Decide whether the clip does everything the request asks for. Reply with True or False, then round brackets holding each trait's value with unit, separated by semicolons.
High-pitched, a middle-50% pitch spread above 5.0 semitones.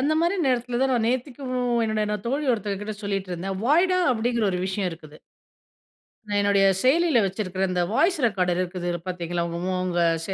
True (210 Hz; 5.6 semitones)